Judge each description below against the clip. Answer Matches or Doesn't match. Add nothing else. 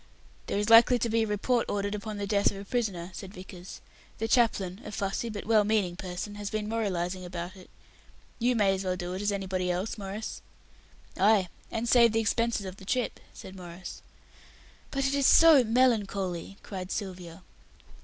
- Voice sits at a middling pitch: Doesn't match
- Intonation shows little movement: Doesn't match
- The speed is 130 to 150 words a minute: Doesn't match